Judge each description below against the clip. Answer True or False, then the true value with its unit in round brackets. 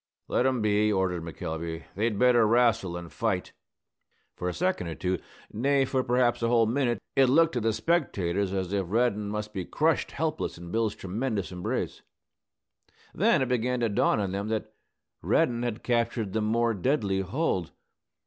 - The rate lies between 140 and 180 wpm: True (170 wpm)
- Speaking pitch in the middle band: False (110 Hz)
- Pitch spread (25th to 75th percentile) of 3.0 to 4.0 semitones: False (4.4 semitones)